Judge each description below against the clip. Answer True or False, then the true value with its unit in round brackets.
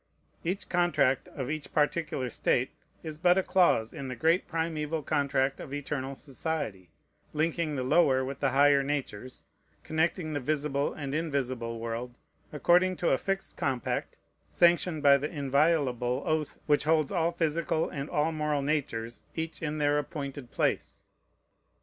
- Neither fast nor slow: True (150 wpm)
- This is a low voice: False (145 Hz)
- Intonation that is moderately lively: True (3.1 semitones)